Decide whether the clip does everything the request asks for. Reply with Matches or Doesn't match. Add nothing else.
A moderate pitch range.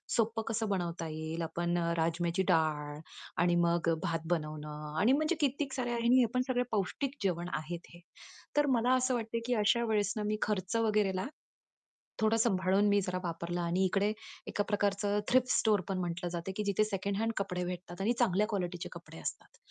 Matches